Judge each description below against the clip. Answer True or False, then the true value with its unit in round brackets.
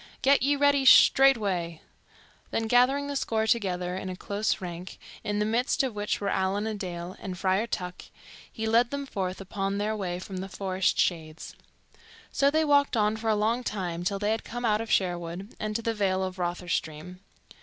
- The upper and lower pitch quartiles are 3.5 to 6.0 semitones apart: True (3.8 semitones)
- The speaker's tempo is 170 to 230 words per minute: True (195 wpm)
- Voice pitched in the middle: False (205 Hz)